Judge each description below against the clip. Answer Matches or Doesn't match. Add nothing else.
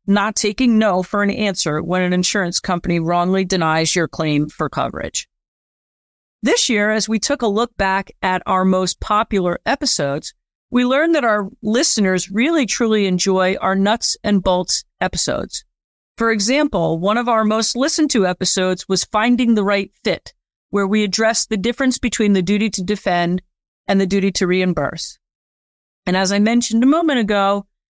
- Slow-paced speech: Doesn't match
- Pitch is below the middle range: Doesn't match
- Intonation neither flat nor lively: Matches